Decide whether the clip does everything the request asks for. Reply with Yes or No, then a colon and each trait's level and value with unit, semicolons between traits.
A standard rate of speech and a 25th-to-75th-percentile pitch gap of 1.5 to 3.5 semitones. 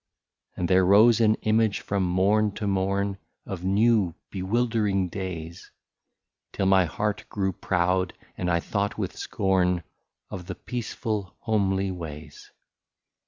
No: slow, 125 wpm; narrow, 2.5 semitones